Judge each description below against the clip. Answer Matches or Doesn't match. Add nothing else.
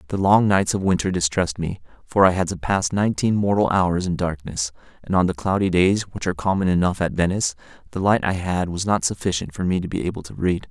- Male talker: Matches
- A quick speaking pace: Matches